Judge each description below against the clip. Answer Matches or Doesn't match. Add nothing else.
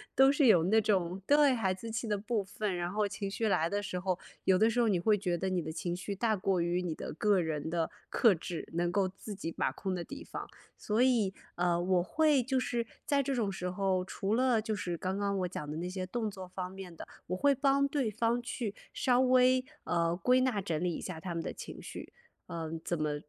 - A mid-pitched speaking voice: Doesn't match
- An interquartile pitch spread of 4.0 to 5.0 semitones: Matches